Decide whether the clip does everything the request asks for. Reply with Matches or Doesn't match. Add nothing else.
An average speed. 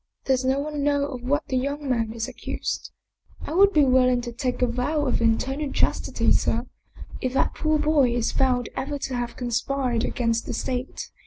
Doesn't match